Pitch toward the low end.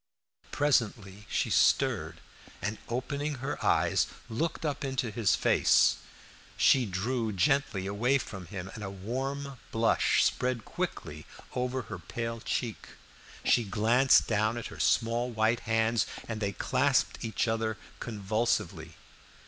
Yes: low, 115 Hz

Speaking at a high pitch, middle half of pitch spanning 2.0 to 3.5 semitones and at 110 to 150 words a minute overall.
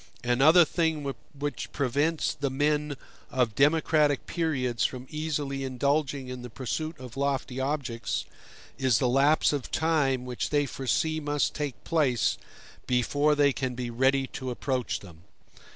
No: medium, 140 Hz; average, 2.8 semitones; average, 140 wpm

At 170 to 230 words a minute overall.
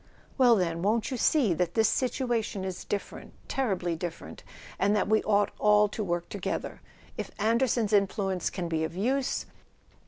No: average, 155 wpm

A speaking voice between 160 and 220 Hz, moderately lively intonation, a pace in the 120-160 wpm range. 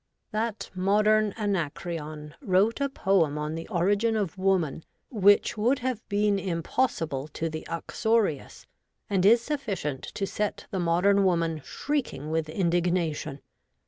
Yes: high, 190 Hz; average, 4.7 semitones; slow, 135 wpm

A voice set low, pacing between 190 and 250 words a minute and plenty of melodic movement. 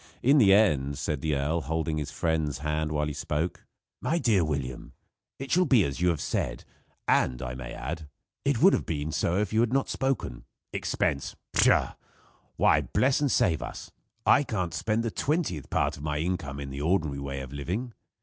Yes: very low, 80 Hz; average, 195 wpm; wide, 7.4 semitones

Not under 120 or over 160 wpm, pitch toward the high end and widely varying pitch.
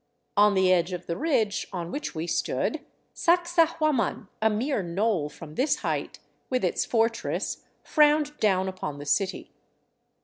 Yes: average, 145 wpm; high, 210 Hz; wide, 8.4 semitones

